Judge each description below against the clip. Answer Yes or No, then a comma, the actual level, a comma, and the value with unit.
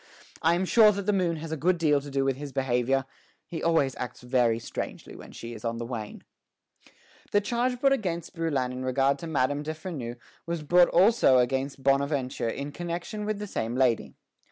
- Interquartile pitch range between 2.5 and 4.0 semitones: No, average, 5.2 semitones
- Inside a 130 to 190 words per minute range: No, average, 200 wpm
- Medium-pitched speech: Yes, medium, 145 Hz